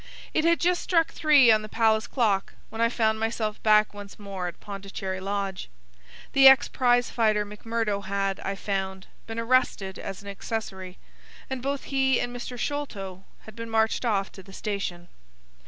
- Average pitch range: Yes, average, 3.7 semitones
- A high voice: Yes, high, 215 Hz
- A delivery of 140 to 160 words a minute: No, average, 170 wpm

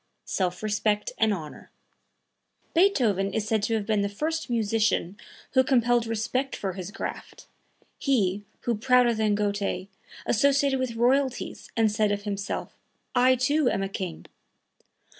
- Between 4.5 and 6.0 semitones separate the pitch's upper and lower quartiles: No, average, 3.7 semitones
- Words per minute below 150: Yes, average, 140 wpm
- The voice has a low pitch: No, high, 220 Hz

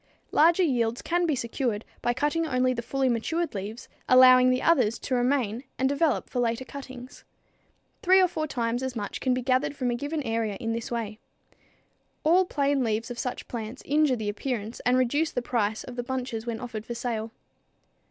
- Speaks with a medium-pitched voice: No, very high, 250 Hz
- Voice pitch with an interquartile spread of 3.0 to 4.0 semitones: Yes, average, 3.4 semitones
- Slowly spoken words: No, average, 190 wpm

